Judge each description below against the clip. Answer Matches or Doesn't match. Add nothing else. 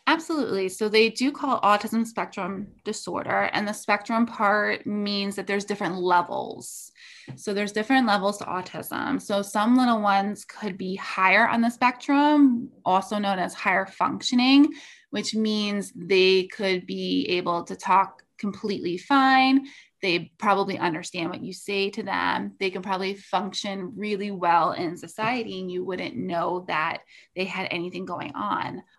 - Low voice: Doesn't match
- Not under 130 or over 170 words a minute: Matches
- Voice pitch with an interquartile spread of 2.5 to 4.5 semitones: Matches